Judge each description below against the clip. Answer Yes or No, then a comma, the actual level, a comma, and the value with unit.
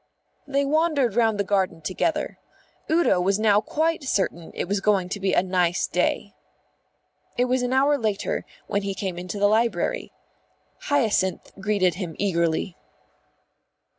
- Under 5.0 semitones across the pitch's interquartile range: No, wide, 5.5 semitones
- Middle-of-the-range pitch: No, high, 205 Hz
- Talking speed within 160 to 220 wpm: No, average, 145 wpm